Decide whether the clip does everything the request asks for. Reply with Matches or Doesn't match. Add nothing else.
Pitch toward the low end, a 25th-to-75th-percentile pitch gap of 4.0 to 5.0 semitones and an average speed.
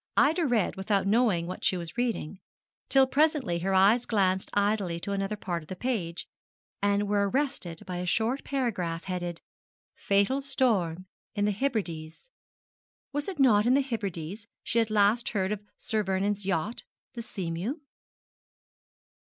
Doesn't match